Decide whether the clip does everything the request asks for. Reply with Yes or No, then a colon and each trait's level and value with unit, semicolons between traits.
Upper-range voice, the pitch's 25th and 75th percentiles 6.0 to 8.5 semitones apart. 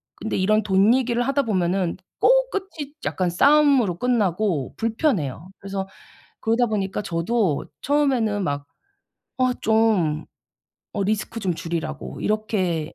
No: high, 210 Hz; wide, 5.4 semitones